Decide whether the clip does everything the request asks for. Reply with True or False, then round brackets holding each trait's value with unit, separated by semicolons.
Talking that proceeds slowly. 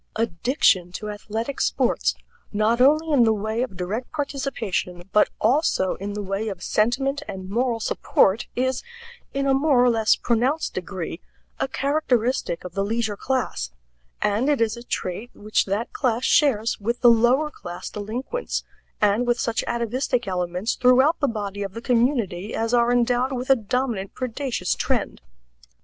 False (160 wpm)